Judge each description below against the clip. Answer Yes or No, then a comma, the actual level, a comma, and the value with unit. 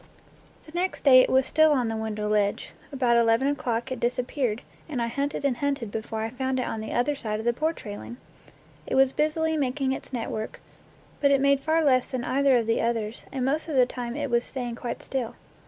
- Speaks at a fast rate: Yes, fast, 220 wpm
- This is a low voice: No, very high, 255 Hz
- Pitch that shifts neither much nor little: Yes, average, 3.2 semitones